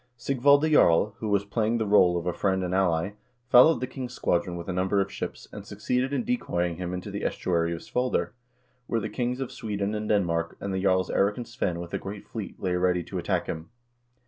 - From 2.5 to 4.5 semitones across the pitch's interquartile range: No, average, 5.2 semitones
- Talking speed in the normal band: No, fast, 225 wpm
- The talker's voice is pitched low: Yes, low, 100 Hz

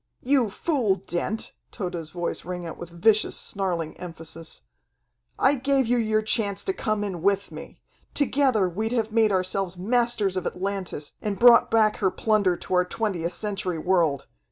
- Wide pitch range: No, average, 3.8 semitones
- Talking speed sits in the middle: Yes, average, 160 wpm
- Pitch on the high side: Yes, high, 200 Hz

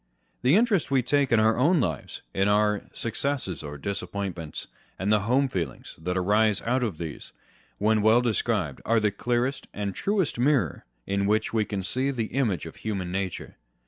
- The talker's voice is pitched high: No, low, 110 Hz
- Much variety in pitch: No, average, 4.6 semitones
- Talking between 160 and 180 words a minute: Yes, average, 175 wpm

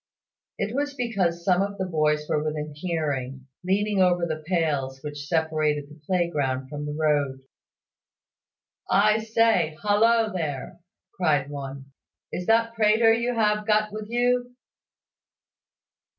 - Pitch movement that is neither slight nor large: No, wide, 6.2 semitones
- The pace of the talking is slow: Yes, slow, 130 wpm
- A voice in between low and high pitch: Yes, medium, 175 Hz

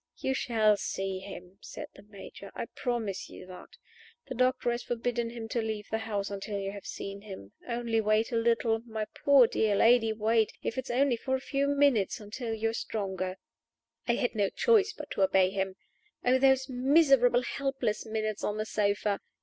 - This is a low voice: No, high, 225 Hz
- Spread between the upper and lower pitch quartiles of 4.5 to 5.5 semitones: No, average, 3.4 semitones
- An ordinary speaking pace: Yes, average, 190 wpm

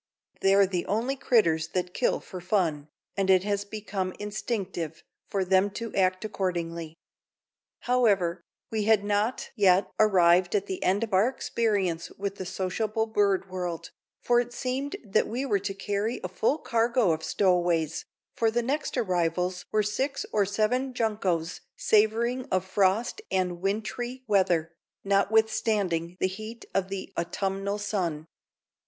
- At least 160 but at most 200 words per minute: No, average, 145 wpm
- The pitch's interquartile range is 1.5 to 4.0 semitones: Yes, average, 3.2 semitones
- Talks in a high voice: Yes, high, 200 Hz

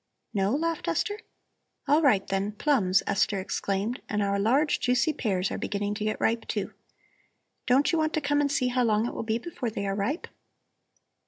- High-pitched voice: Yes, high, 230 Hz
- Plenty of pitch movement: Yes, wide, 6.2 semitones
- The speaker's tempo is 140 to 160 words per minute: No, average, 190 wpm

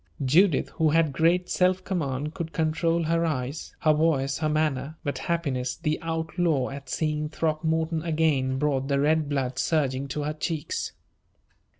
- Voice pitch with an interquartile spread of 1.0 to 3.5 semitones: Yes, average, 2.8 semitones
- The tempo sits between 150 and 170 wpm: Yes, average, 155 wpm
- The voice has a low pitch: No, medium, 155 Hz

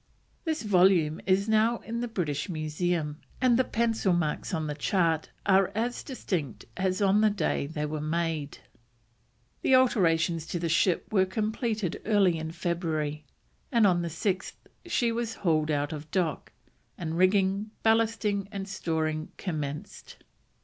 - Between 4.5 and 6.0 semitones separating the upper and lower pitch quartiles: Yes, average, 5.0 semitones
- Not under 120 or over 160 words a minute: Yes, average, 150 wpm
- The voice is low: No, medium, 180 Hz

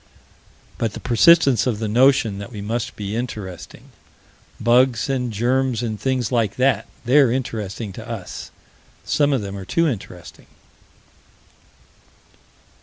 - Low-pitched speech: Yes, low, 120 Hz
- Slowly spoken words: Yes, slow, 130 wpm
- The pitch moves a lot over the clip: No, average, 3.7 semitones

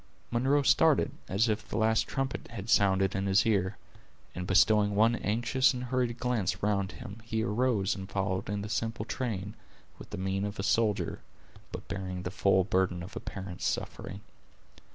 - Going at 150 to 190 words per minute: Yes, average, 175 wpm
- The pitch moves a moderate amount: Yes, average, 3.1 semitones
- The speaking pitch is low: Yes, low, 105 Hz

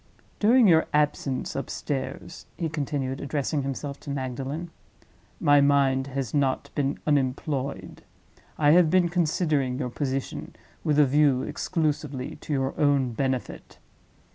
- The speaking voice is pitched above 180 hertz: No, medium, 140 Hz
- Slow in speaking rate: Yes, slow, 125 wpm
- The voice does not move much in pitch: Yes, narrow, 2.2 semitones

